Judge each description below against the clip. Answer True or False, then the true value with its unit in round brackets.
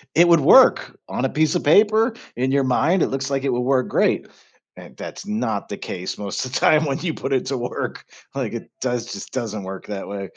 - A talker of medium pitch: False (130 Hz)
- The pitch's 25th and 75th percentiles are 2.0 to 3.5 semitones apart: False (5.4 semitones)